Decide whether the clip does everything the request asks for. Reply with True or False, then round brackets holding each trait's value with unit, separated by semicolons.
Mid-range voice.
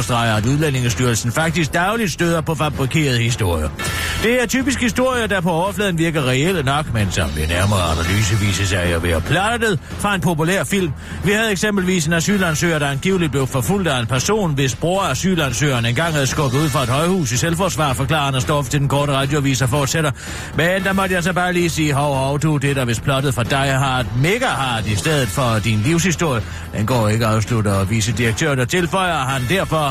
True (145 Hz)